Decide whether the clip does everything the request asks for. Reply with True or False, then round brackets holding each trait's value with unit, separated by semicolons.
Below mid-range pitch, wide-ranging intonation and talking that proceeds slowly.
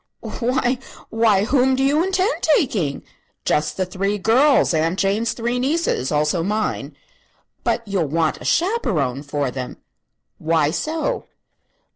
False (210 Hz; 8.6 semitones; 130 wpm)